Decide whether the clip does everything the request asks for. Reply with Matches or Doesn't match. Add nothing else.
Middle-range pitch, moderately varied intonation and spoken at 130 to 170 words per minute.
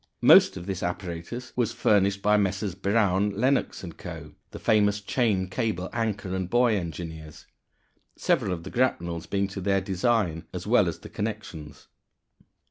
Doesn't match